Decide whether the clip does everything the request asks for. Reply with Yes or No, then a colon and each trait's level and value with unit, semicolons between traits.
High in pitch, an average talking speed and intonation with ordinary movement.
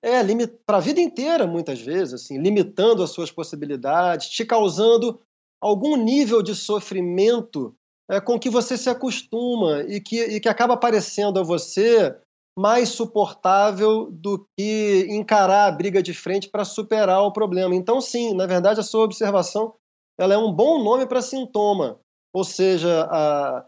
Yes: high, 210 Hz; average, 160 wpm; average, 3.6 semitones